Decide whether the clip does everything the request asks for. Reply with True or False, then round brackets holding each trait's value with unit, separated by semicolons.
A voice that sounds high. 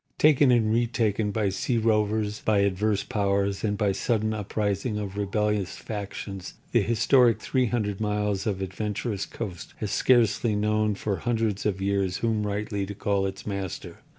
False (105 Hz)